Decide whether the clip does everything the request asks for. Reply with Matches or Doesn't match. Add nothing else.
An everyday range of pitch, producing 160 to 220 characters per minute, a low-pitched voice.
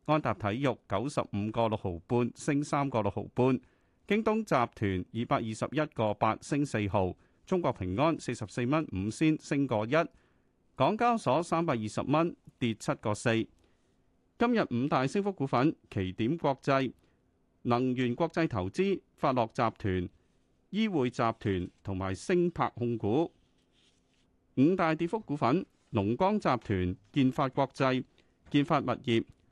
Doesn't match